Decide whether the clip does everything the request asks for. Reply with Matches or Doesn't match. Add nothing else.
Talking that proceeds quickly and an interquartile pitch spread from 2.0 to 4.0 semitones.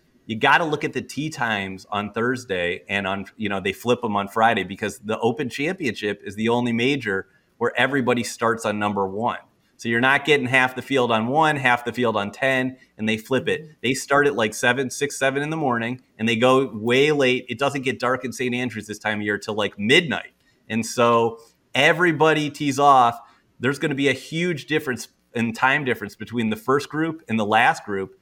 Matches